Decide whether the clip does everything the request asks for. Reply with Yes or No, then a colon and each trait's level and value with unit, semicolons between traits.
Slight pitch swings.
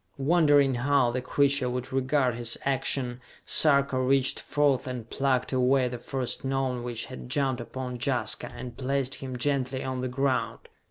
Yes: narrow, 1.7 semitones